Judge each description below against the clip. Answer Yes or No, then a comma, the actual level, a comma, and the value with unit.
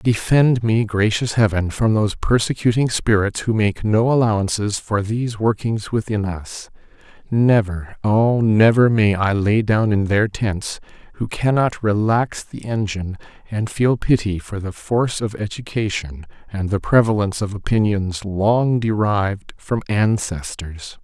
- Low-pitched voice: Yes, low, 105 Hz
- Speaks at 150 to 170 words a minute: No, slow, 135 wpm